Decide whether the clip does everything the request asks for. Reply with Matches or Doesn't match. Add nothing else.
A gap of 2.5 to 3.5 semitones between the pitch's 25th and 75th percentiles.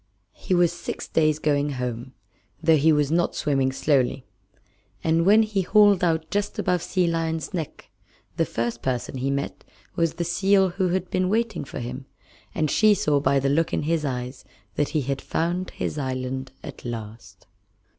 Doesn't match